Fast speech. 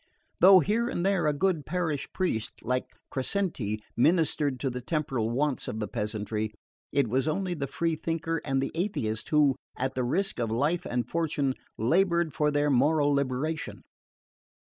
No: average, 165 wpm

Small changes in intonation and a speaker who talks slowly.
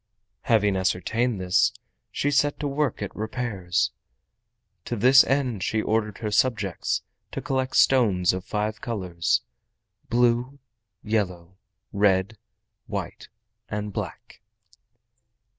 No: average, 4.4 semitones; slow, 105 wpm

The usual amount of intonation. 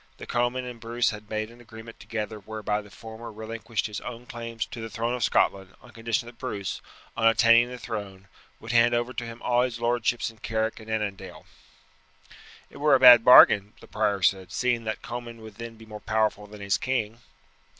No: narrow, 1.9 semitones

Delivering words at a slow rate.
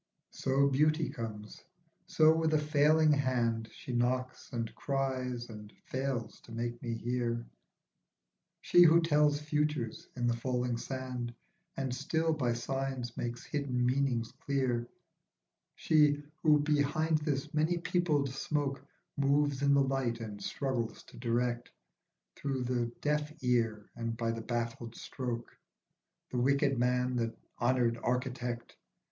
Yes: slow, 130 wpm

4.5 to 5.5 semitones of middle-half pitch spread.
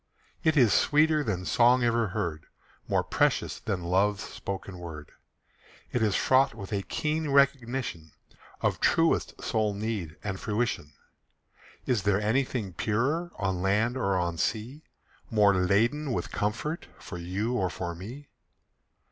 Yes: average, 5.0 semitones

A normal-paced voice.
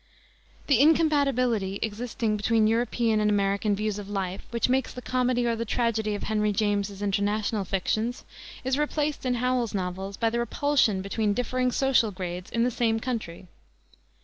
Yes: average, 160 wpm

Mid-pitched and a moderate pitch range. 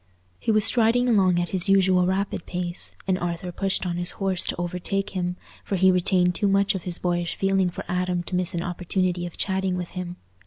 No: medium, 180 Hz; narrow, 1.7 semitones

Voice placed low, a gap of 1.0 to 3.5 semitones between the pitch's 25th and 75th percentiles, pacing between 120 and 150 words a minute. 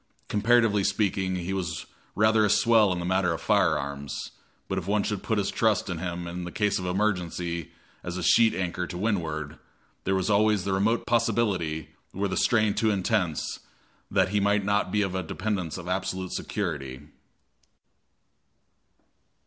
No: very low, 95 Hz; average, 3.0 semitones; average, 160 wpm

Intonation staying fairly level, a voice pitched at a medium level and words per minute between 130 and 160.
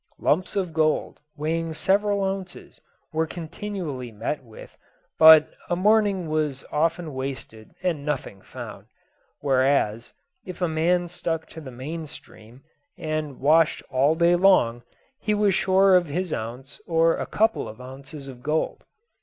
No: average, 4.7 semitones; medium, 160 Hz; average, 140 wpm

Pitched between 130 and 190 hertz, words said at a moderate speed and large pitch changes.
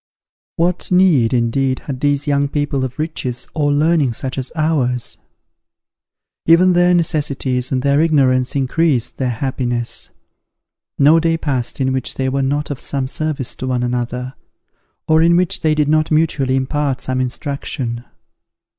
No: medium, 140 Hz; average, 150 wpm; average, 3.3 semitones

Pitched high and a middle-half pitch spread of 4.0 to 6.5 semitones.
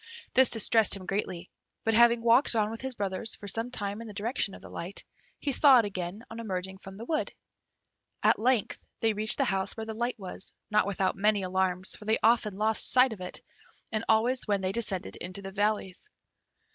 No: high, 215 Hz; average, 3.1 semitones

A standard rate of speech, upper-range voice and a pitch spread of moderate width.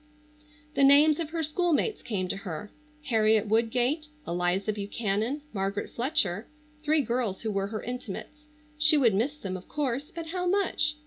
No: average, 155 wpm; high, 240 Hz; wide, 6.9 semitones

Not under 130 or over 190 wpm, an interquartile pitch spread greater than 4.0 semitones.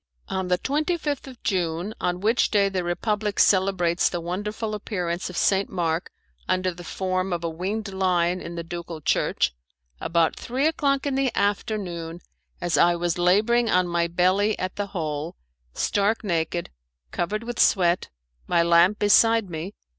No: average, 160 wpm; average, 3.5 semitones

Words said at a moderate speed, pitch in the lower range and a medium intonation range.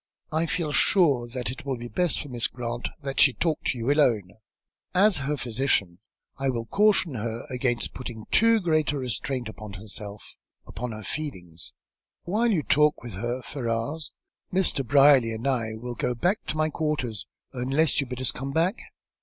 Yes: average, 180 wpm; low, 130 Hz; average, 4.8 semitones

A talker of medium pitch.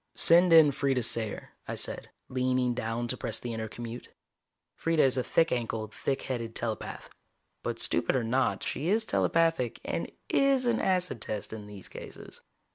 No: low, 125 Hz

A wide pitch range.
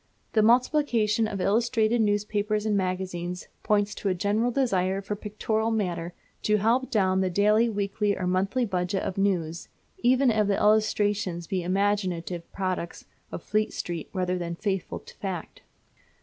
No: average, 2.8 semitones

